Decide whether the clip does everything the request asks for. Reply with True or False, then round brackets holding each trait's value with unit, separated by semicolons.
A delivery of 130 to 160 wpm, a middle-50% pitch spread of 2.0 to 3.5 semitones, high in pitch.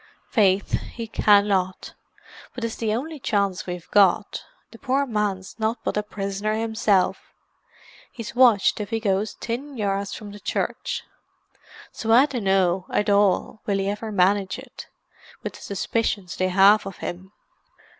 True (150 wpm; 2.5 semitones; 205 Hz)